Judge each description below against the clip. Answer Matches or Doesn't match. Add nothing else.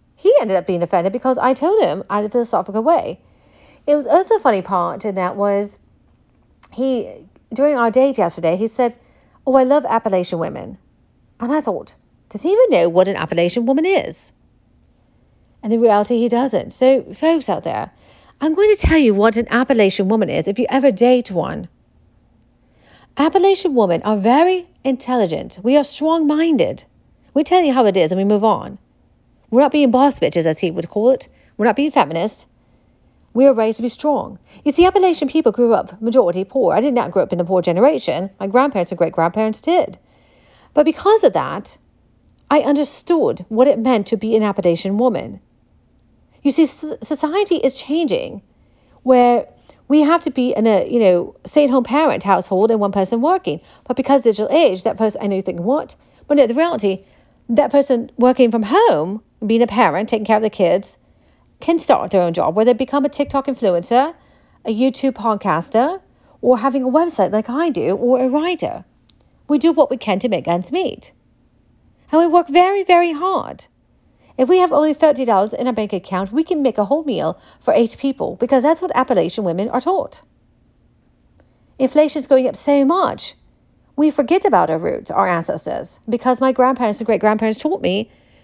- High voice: Matches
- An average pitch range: Doesn't match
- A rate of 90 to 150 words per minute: Doesn't match